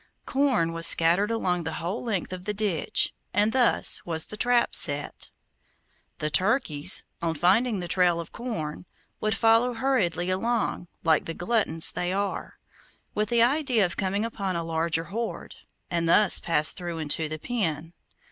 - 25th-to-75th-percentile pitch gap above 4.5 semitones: Yes, average, 5.3 semitones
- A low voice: No, medium, 185 Hz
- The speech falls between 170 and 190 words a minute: No, average, 160 wpm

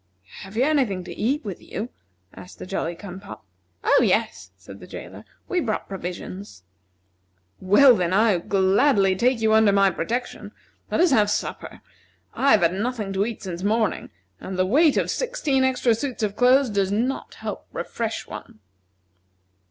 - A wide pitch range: No, average, 4.9 semitones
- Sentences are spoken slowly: No, average, 175 wpm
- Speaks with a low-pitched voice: No, high, 210 Hz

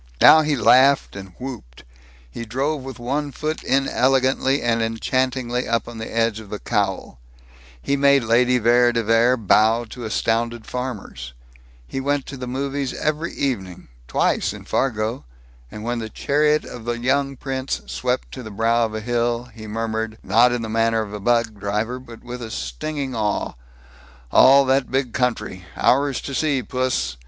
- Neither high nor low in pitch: No, low, 120 Hz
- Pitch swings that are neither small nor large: Yes, average, 3.1 semitones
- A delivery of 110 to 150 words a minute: No, average, 170 wpm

